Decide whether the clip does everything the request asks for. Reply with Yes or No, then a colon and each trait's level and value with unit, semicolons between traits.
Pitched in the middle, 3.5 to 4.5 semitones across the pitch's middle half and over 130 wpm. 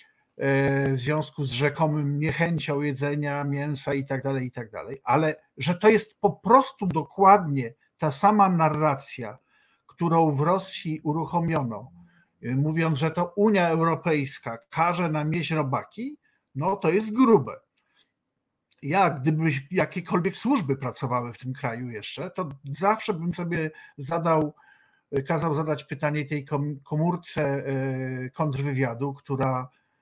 No: medium, 155 Hz; average, 4.0 semitones; average, 120 wpm